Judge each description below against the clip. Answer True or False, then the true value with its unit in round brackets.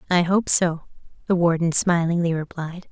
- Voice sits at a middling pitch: True (170 Hz)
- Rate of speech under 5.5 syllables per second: True (4.8 syllables/s)